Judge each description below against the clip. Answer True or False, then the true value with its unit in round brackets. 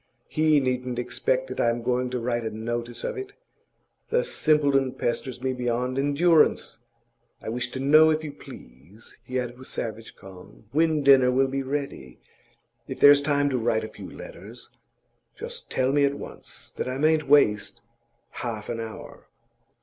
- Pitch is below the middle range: True (130 Hz)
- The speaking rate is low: False (165 wpm)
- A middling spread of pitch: True (3.4 semitones)